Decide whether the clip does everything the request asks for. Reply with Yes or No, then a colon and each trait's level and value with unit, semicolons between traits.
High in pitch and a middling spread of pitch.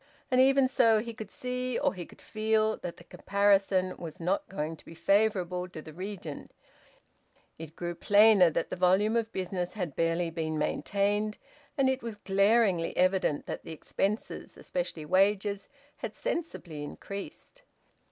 Yes: high, 195 Hz; average, 4.0 semitones